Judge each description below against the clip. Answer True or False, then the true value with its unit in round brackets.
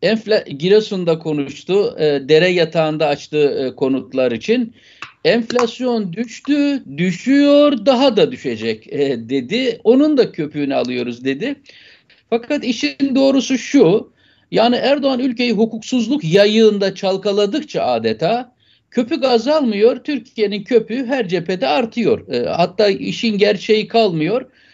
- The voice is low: False (220 Hz)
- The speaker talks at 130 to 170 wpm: False (110 wpm)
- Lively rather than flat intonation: True (7.4 semitones)